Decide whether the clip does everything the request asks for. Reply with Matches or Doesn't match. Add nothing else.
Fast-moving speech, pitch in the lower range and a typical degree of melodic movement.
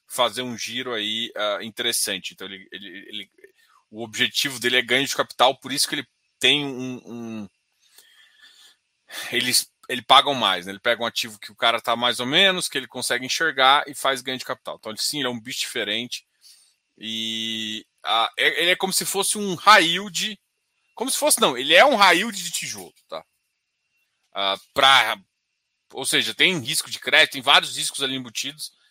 Doesn't match